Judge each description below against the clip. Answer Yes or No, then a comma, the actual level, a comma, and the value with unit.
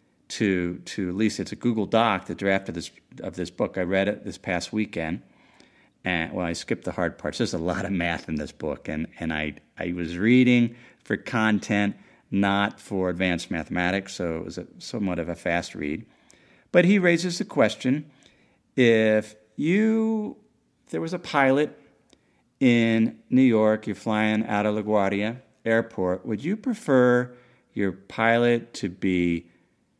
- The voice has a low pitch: Yes, low, 110 Hz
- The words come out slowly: No, average, 165 wpm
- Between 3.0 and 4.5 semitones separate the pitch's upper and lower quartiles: No, average, 4.9 semitones